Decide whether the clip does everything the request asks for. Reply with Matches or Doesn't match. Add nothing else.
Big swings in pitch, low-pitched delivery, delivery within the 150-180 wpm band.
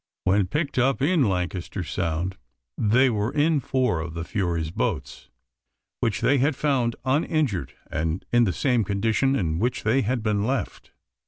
Matches